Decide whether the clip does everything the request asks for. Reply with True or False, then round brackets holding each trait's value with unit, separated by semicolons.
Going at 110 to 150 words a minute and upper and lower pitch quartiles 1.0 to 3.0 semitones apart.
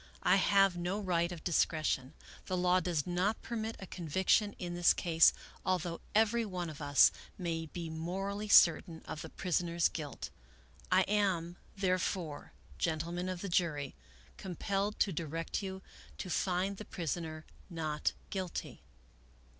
True (140 wpm; 2.6 semitones)